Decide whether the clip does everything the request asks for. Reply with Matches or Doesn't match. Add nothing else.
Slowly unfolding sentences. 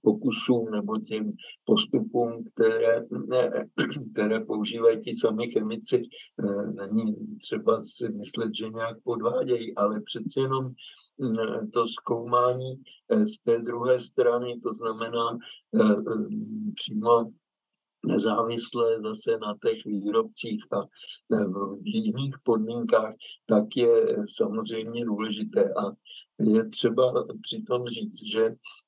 Matches